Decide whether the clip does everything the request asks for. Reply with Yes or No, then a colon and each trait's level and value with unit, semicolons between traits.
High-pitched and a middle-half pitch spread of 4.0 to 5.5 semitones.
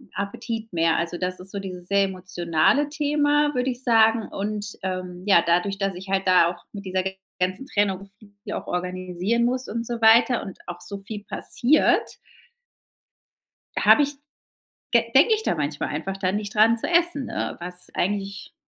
Yes: high, 200 Hz; average, 4.3 semitones